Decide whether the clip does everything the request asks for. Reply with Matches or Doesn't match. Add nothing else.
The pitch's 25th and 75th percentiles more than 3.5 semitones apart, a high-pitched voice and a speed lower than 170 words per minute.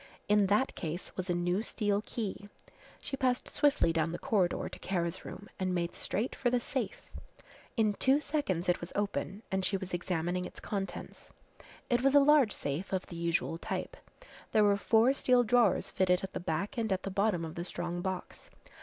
Doesn't match